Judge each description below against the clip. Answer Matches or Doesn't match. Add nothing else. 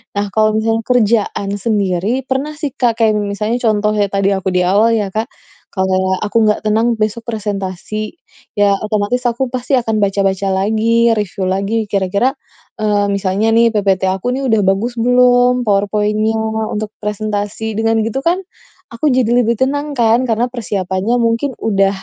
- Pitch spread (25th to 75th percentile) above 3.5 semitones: Doesn't match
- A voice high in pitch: Matches